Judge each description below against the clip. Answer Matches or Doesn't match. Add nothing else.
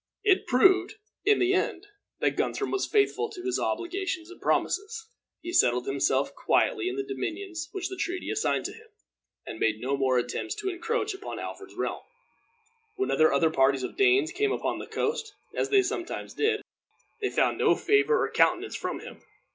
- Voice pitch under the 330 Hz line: Doesn't match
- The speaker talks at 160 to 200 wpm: Matches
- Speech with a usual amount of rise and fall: Matches